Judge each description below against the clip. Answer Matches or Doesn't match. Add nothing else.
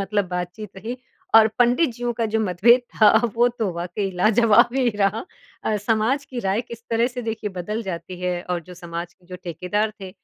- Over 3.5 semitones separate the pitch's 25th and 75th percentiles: Matches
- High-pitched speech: Matches